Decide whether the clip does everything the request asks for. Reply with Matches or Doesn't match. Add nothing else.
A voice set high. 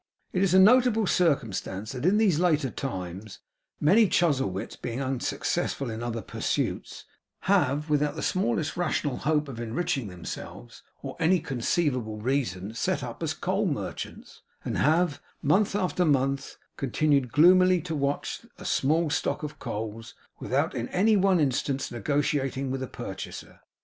Doesn't match